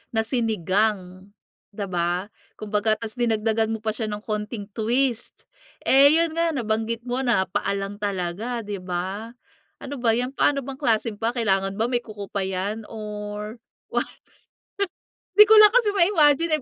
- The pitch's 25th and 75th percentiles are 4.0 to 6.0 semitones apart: No, average, 3.3 semitones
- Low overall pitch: No, high, 220 Hz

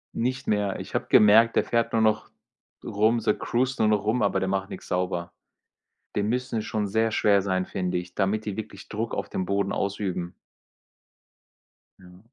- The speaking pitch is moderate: No, low, 105 Hz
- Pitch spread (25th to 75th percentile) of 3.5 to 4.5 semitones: No, narrow, 2.6 semitones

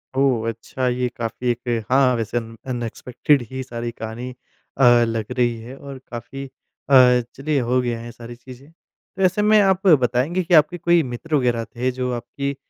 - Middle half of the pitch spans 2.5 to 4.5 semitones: Yes, average, 2.8 semitones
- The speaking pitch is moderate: No, low, 125 Hz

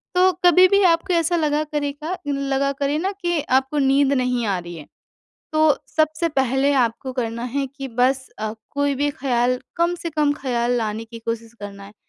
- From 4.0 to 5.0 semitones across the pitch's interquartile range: Yes, average, 4.4 semitones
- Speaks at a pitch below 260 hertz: No, very high, 275 Hz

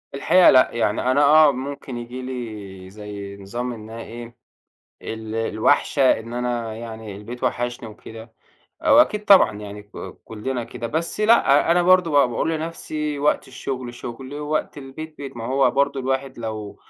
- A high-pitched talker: No, low, 125 Hz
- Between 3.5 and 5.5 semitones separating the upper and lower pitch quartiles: Yes, average, 4.2 semitones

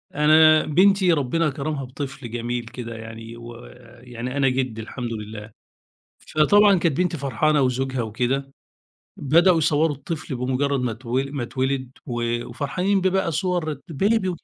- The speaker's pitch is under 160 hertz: Yes, low, 135 Hz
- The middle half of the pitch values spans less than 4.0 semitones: No, average, 4.6 semitones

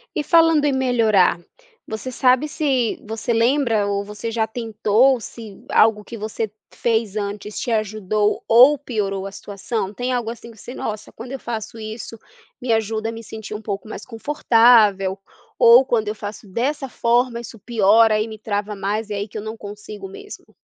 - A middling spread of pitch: No, narrow, 2.3 semitones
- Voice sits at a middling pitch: No, high, 220 Hz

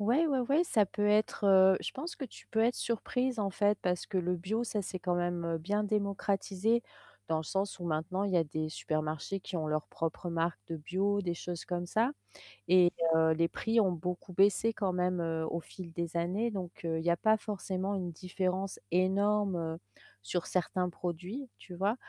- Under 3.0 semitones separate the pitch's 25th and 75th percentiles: No, average, 3.3 semitones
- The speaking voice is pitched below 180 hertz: No, medium, 185 Hz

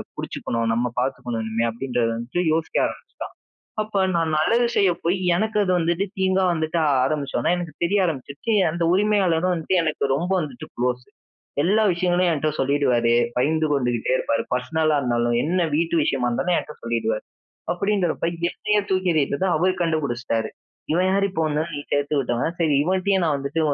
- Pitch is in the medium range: Yes, medium, 160 Hz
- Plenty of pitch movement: Yes, wide, 6.2 semitones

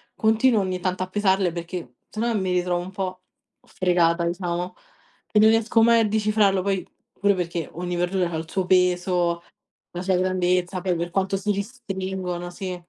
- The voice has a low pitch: No, medium, 185 Hz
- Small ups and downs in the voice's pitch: Yes, narrow, 2.0 semitones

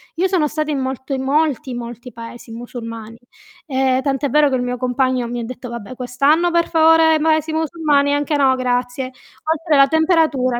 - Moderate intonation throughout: Yes, average, 4.0 semitones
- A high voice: Yes, very high, 270 Hz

